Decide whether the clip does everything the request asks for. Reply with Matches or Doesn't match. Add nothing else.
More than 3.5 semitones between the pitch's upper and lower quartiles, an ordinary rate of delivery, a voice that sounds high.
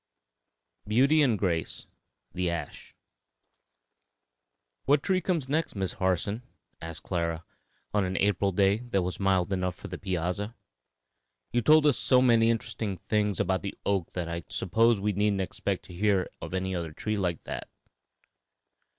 Doesn't match